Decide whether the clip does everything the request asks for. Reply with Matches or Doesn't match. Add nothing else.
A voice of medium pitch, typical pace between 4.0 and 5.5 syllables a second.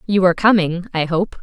Doesn't match